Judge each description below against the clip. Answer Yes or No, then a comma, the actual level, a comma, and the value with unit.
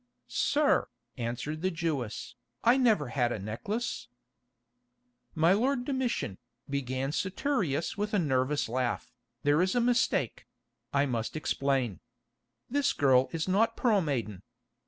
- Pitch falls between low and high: Yes, medium, 150 Hz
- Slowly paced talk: Yes, slow, 120 wpm